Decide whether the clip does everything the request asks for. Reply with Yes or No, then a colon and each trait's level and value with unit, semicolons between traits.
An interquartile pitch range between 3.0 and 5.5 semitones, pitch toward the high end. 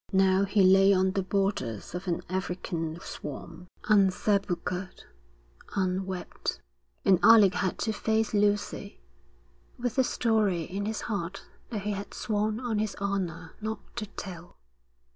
No: narrow, 2.5 semitones; high, 195 Hz